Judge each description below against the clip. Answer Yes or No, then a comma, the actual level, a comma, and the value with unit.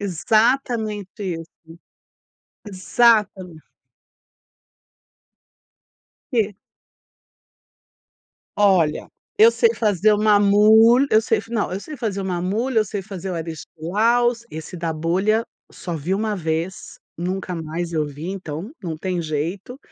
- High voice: Yes, high, 195 Hz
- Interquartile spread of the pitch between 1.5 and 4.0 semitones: No, average, 4.5 semitones